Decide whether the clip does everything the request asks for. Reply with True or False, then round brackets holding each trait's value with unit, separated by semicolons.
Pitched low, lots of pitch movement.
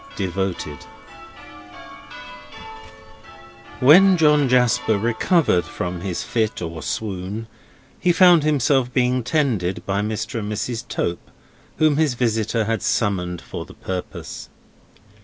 True (115 Hz; 5.7 semitones)